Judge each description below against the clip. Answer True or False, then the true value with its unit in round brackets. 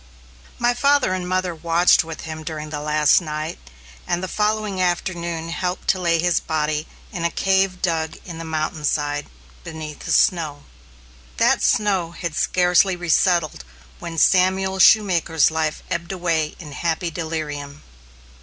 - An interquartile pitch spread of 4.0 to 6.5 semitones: False (2.8 semitones)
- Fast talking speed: False (145 wpm)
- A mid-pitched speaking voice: True (170 Hz)